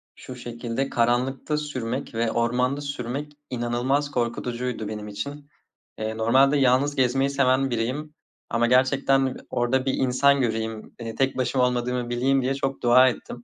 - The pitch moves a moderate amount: No, narrow, 2.3 semitones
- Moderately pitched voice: No, low, 125 Hz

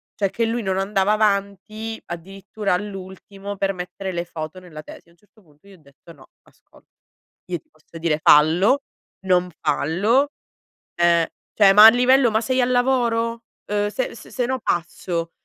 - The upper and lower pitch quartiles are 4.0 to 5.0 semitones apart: Yes, average, 4.4 semitones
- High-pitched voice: Yes, high, 195 Hz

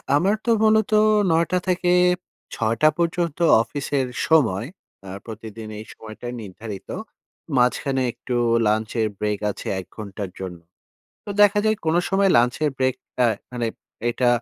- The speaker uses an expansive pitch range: Yes, wide, 7.6 semitones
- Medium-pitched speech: No, low, 125 Hz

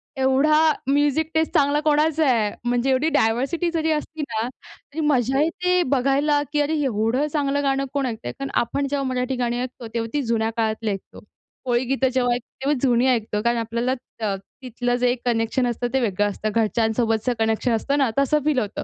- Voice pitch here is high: Yes, very high, 255 Hz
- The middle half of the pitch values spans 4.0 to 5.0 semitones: No, average, 3.5 semitones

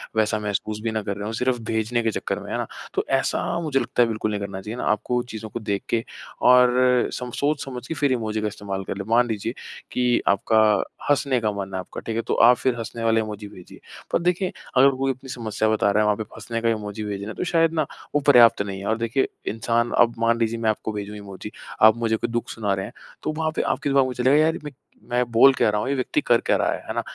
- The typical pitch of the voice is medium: No, low, 115 Hz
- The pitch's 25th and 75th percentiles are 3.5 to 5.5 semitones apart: No, average, 3.0 semitones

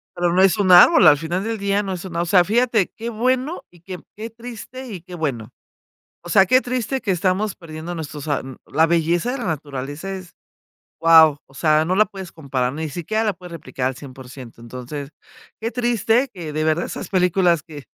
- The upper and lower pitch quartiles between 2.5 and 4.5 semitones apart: No, wide, 5.5 semitones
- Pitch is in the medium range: Yes, medium, 175 Hz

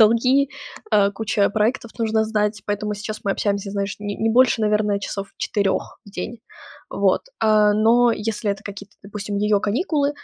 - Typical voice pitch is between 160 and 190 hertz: No, high, 210 Hz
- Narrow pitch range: Yes, narrow, 1.7 semitones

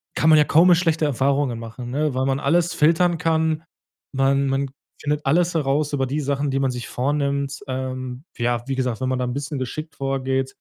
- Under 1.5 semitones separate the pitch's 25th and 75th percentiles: No, average, 2.7 semitones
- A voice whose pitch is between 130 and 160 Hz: Yes, medium, 140 Hz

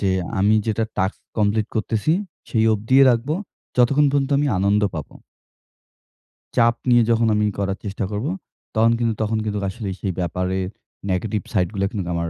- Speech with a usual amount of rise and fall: Yes, average, 3.0 semitones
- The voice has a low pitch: Yes, low, 105 Hz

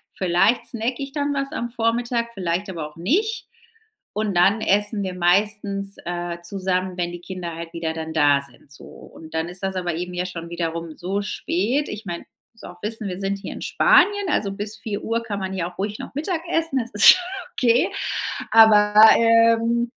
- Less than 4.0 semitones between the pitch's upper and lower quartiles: No, average, 4.7 semitones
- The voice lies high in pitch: Yes, high, 200 Hz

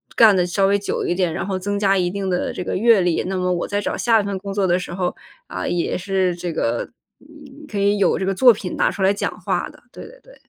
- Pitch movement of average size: No, narrow, 2.1 semitones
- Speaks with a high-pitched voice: Yes, high, 195 Hz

